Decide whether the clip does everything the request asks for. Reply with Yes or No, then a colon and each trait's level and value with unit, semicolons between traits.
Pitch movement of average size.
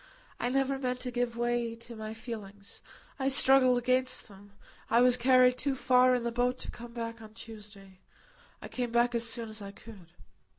No: narrow, 2.2 semitones